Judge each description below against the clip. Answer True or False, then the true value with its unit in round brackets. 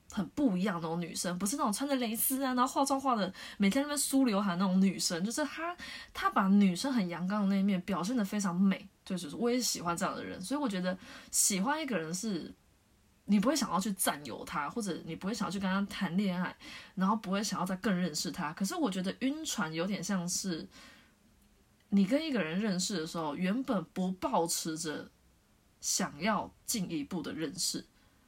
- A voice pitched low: False (200 Hz)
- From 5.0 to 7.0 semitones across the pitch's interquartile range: True (5.5 semitones)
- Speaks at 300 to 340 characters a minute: True (310 characters per minute)